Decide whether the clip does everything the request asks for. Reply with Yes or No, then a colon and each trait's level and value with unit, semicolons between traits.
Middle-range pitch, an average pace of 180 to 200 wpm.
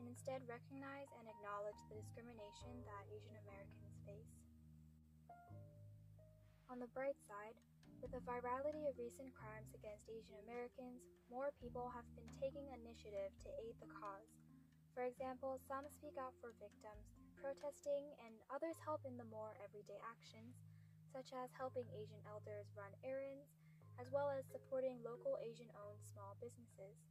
No: medium, 155 Hz; average, 145 wpm